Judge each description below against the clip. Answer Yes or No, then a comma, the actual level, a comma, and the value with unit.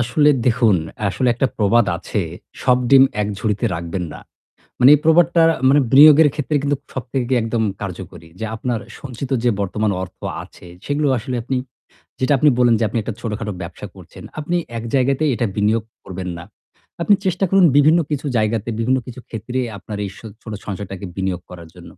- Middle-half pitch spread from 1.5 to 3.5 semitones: No, average, 5.0 semitones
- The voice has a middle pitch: No, low, 120 Hz